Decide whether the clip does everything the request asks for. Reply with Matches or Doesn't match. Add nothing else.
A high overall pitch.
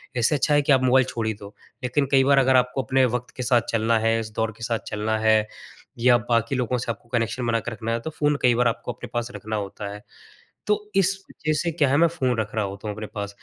Doesn't match